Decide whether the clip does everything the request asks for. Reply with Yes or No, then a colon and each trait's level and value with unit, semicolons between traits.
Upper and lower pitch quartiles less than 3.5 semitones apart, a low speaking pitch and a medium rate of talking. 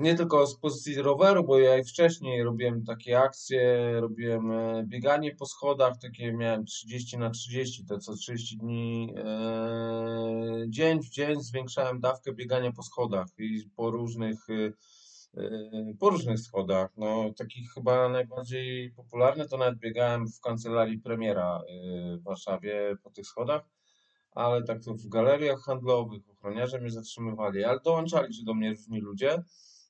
Yes: average, 2.8 semitones; low, 120 Hz; average, 145 wpm